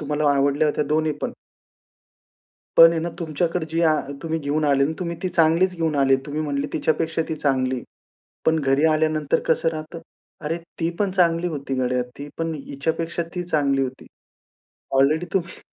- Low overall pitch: No, medium, 155 Hz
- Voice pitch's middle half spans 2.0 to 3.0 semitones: Yes, average, 2.7 semitones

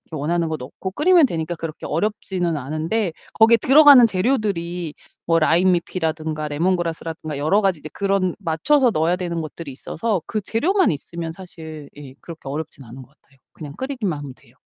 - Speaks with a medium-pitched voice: Yes, medium, 170 Hz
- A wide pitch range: No, average, 4.4 semitones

